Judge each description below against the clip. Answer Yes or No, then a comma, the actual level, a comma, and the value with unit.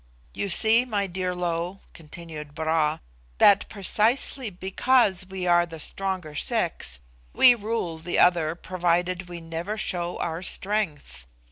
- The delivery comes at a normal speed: No, slow, 130 wpm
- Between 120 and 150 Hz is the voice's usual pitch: No, medium, 180 Hz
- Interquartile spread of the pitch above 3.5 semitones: No, average, 3.2 semitones